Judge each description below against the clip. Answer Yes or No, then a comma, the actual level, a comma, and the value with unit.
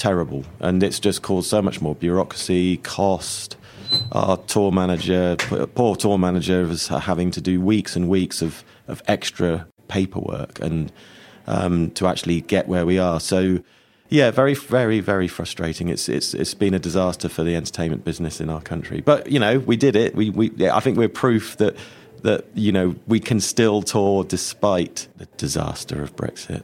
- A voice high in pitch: No, very low, 95 Hz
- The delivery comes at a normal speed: Yes, average, 180 wpm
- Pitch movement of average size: Yes, average, 3.5 semitones